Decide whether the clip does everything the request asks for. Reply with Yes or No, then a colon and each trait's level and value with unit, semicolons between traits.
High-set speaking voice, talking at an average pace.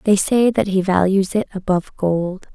Yes: high, 195 Hz; average, 190 wpm